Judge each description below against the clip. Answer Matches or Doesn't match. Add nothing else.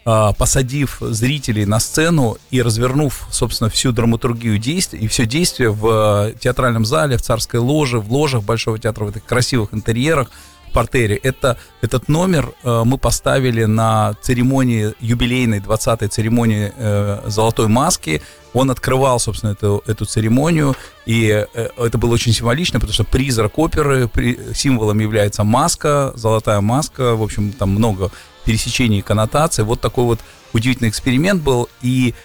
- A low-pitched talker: Matches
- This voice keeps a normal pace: Matches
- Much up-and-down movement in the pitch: Doesn't match